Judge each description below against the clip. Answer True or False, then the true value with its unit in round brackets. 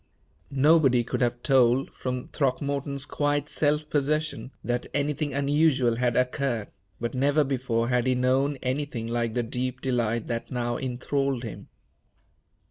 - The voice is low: True (130 Hz)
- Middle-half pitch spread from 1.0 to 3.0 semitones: True (2.7 semitones)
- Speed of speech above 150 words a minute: False (135 wpm)